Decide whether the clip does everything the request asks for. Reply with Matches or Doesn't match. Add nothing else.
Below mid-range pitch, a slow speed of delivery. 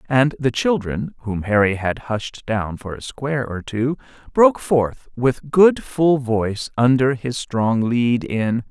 Doesn't match